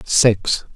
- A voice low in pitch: Yes, low, 105 Hz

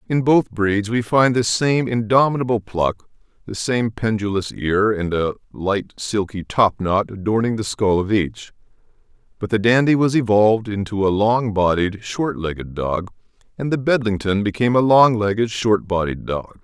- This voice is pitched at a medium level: No, low, 110 Hz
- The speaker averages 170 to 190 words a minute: No, average, 160 wpm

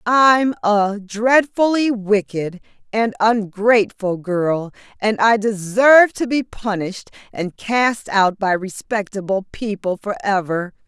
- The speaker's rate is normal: No, slow, 110 wpm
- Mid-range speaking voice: No, high, 210 Hz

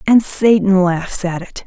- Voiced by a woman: Yes, female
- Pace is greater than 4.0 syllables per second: No, 3.9 syllables/s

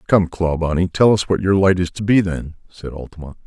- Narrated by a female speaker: No, male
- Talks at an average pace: No, fast, 225 wpm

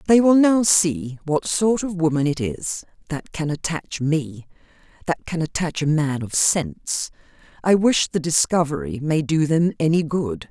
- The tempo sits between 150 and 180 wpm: Yes, average, 170 wpm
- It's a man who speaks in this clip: No, female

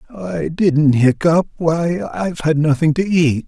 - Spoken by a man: Yes, male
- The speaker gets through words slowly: No, average, 155 wpm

